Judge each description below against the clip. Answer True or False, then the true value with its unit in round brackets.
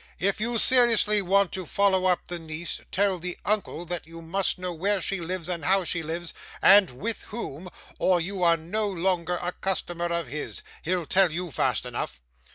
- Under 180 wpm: False (190 wpm)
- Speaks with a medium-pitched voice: True (180 Hz)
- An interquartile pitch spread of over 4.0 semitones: False (2.6 semitones)